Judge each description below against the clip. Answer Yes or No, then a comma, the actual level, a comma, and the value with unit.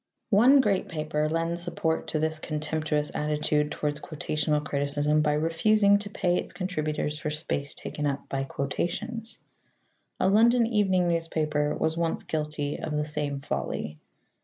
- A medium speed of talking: Yes, average, 145 wpm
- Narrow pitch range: No, average, 3.0 semitones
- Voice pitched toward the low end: No, medium, 155 Hz